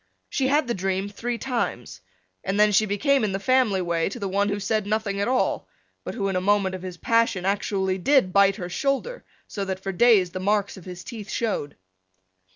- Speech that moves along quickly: Yes, fast, 210 wpm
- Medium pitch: No, high, 200 Hz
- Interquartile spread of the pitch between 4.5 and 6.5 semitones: No, average, 3.3 semitones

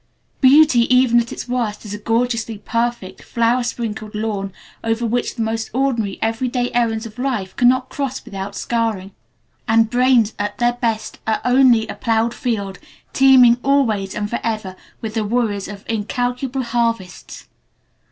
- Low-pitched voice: No, high, 230 Hz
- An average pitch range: No, narrow, 2.3 semitones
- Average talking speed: Yes, average, 150 wpm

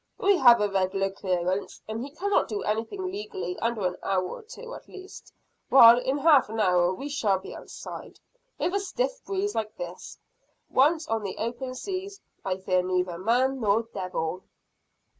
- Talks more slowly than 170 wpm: No, average, 175 wpm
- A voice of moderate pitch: No, high, 230 Hz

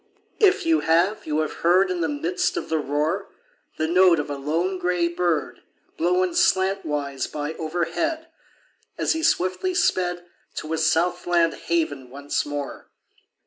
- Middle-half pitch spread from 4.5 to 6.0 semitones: No, average, 3.2 semitones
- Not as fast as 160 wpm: Yes, average, 150 wpm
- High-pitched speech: No, medium, 170 Hz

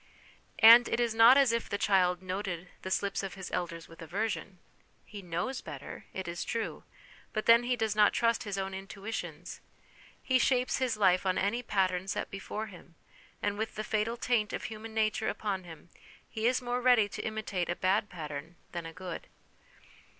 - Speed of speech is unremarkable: Yes, average, 185 wpm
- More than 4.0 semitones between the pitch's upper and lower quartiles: No, average, 3.5 semitones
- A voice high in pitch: Yes, high, 205 Hz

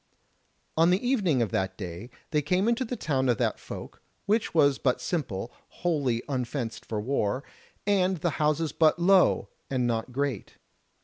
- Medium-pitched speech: Yes, medium, 145 Hz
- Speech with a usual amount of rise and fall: No, wide, 6.7 semitones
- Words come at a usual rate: Yes, average, 165 wpm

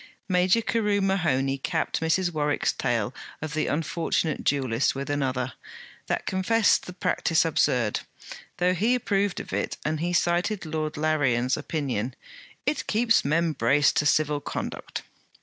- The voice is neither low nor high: Yes, medium, 155 Hz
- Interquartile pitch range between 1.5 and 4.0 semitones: No, average, 4.4 semitones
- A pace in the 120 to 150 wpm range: Yes, average, 140 wpm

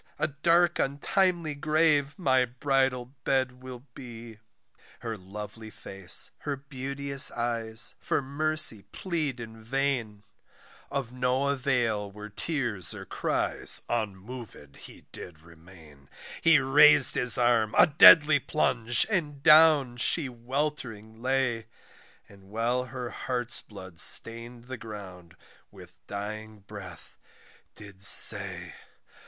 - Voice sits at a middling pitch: No, low, 125 Hz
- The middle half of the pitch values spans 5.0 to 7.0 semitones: No, average, 4.5 semitones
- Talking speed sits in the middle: No, slow, 115 wpm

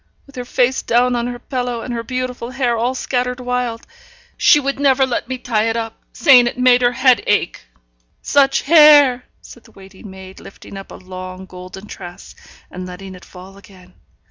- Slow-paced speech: No, average, 190 wpm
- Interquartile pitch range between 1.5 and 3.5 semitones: No, average, 4.7 semitones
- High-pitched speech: Yes, high, 240 Hz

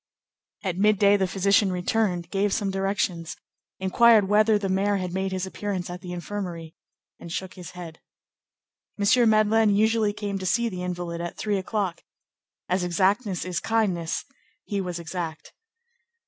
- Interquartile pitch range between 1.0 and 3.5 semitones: Yes, narrow, 2.6 semitones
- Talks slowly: No, average, 150 wpm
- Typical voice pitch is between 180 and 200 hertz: Yes, high, 190 Hz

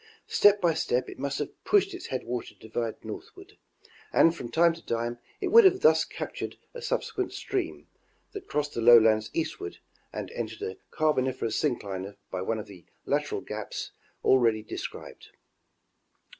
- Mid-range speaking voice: No, low, 130 Hz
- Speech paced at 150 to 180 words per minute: Yes, average, 155 wpm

